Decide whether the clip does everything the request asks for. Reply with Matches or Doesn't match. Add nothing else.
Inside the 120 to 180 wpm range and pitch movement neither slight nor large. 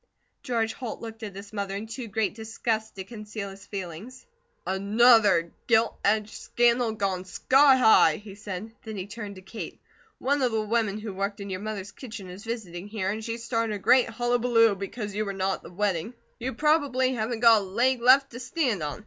Doesn't match